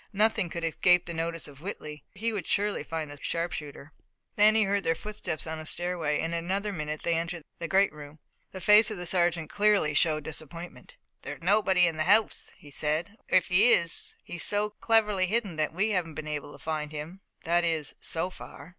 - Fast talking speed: Yes, fast, 210 wpm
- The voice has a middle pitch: Yes, medium, 170 Hz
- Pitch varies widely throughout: No, average, 4.2 semitones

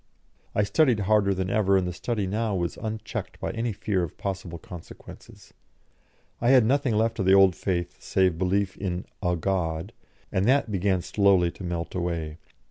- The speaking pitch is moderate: No, very low, 95 Hz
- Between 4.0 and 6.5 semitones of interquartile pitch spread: No, average, 3.3 semitones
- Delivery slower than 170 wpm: No, average, 175 wpm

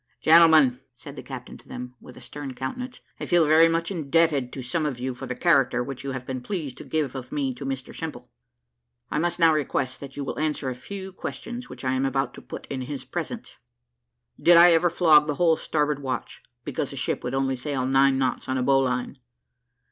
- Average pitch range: Yes, average, 3.8 semitones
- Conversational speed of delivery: No, fast, 220 wpm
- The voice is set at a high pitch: No, medium, 140 Hz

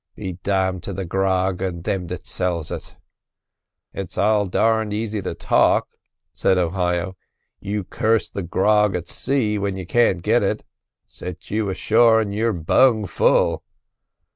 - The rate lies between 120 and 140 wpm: No, average, 150 wpm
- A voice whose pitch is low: Yes, very low, 95 Hz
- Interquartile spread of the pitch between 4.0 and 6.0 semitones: No, average, 2.8 semitones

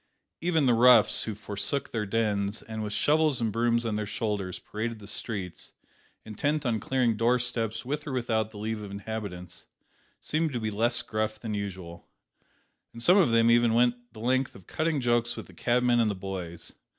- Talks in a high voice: No, low, 115 Hz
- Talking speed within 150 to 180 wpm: No, average, 190 wpm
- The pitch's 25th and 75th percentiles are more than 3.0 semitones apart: No, average, 2.7 semitones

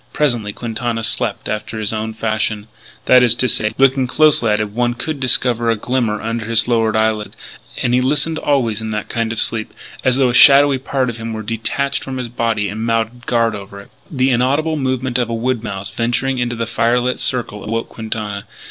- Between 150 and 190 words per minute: No, fast, 205 wpm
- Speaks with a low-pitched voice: Yes, low, 115 Hz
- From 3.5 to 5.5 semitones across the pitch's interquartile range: No, narrow, 2.5 semitones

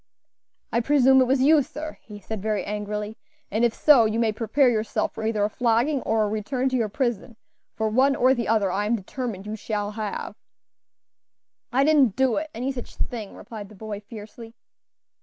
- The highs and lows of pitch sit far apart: No, average, 3.5 semitones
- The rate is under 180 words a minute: No, average, 195 wpm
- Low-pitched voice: No, high, 225 Hz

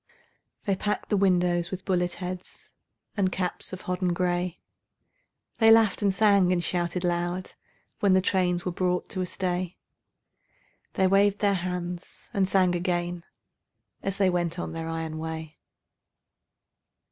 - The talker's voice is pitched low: No, medium, 180 Hz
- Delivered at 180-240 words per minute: No, average, 145 wpm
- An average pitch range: No, narrow, 1.5 semitones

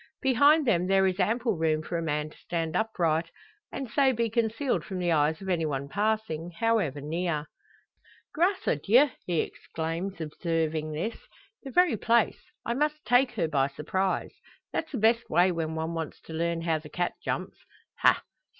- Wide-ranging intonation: Yes, wide, 6.2 semitones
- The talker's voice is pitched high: No, medium, 180 Hz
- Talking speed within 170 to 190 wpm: Yes, average, 175 wpm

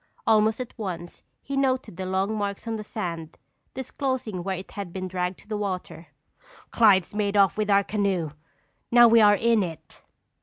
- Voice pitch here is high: Yes, high, 205 Hz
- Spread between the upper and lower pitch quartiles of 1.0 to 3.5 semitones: Yes, average, 3.2 semitones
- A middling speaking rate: Yes, average, 180 wpm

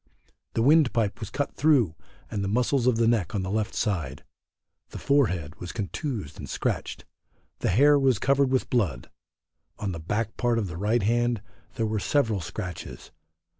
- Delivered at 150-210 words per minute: Yes, average, 170 wpm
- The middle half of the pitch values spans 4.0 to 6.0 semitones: Yes, average, 4.5 semitones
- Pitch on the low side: Yes, low, 110 Hz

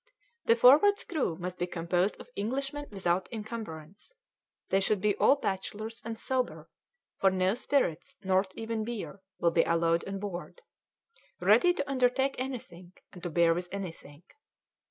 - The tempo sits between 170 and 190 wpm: No, average, 150 wpm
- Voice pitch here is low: No, high, 200 Hz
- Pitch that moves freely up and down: Yes, wide, 5.8 semitones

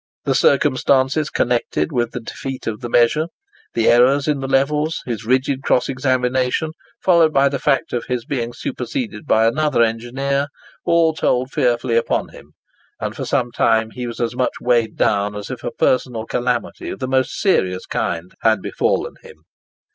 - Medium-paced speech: Yes, average, 170 wpm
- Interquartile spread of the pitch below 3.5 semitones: Yes, average, 2.9 semitones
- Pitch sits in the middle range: No, low, 125 Hz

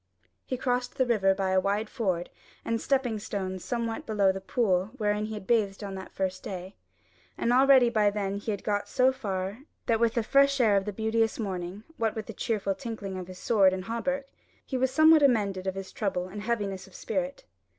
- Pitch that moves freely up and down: No, average, 3.5 semitones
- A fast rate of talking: Yes, fast, 210 wpm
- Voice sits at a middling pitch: No, high, 210 Hz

